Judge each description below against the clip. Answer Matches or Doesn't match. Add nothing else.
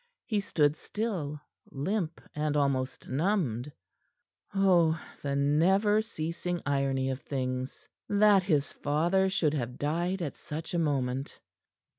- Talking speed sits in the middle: Doesn't match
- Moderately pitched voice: Matches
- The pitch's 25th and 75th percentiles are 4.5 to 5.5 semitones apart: Matches